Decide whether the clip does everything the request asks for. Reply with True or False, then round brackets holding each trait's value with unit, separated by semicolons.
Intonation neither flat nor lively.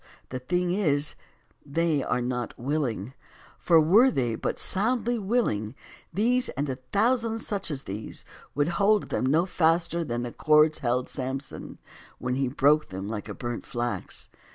False (7.2 semitones)